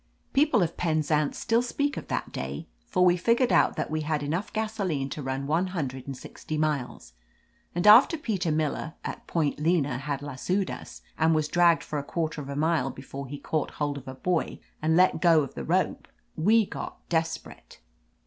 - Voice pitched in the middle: Yes, medium, 155 Hz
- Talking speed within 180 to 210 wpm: Yes, average, 195 wpm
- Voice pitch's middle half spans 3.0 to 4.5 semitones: Yes, average, 4.1 semitones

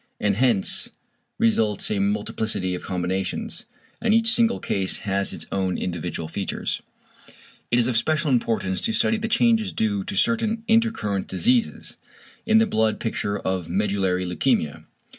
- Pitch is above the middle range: No, low, 105 Hz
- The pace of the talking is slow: No, average, 145 wpm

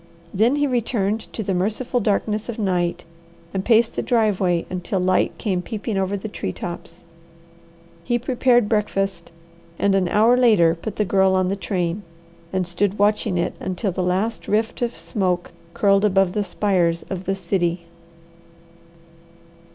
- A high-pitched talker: Yes, high, 195 Hz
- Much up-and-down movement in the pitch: No, average, 3.1 semitones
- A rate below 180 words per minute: Yes, average, 155 wpm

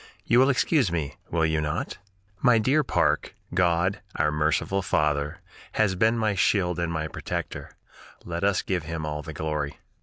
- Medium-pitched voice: No, very low, 85 Hz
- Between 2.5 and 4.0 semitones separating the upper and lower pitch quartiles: No, average, 4.8 semitones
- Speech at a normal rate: Yes, average, 170 wpm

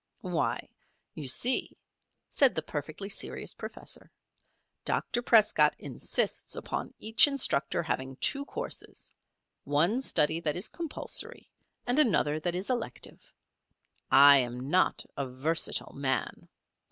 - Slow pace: Yes, slow, 115 wpm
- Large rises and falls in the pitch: Yes, wide, 8.9 semitones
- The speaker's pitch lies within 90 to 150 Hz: No, medium, 165 Hz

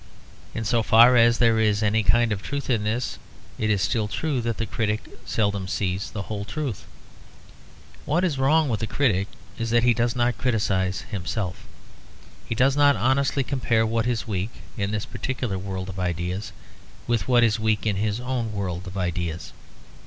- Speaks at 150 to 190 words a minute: Yes, average, 180 wpm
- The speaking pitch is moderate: No, low, 110 Hz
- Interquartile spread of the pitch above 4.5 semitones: No, average, 3.4 semitones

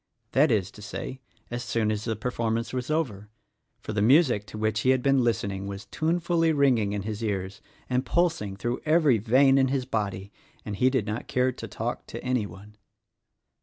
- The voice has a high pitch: No, low, 115 Hz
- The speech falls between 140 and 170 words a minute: No, average, 190 wpm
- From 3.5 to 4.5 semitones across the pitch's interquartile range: Yes, average, 4.2 semitones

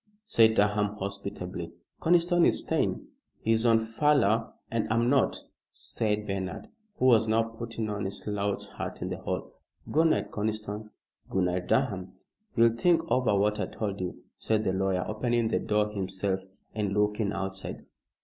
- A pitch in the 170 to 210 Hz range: No, low, 105 Hz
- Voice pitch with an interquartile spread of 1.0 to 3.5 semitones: Yes, narrow, 2.5 semitones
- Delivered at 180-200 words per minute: No, average, 160 wpm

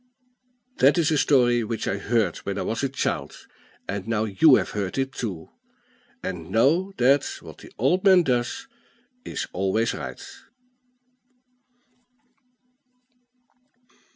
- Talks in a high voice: No, low, 120 Hz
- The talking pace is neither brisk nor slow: No, slow, 125 wpm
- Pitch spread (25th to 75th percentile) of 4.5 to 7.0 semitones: Yes, average, 5.3 semitones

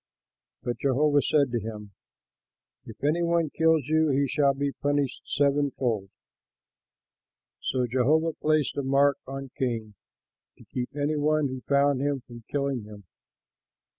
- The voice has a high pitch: No, medium, 140 Hz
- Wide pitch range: No, average, 2.7 semitones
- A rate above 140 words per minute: No, slow, 135 wpm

